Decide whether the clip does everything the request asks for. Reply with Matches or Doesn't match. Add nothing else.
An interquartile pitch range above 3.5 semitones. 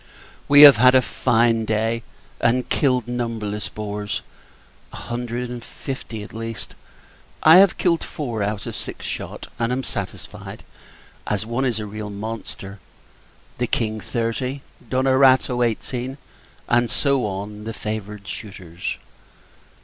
Doesn't match